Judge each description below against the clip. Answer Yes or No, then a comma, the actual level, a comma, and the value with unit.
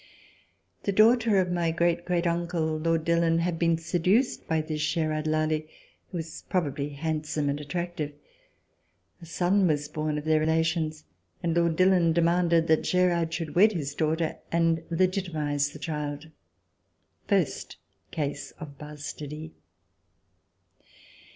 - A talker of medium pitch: Yes, medium, 165 Hz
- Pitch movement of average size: No, narrow, 2.0 semitones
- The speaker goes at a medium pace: No, slow, 130 wpm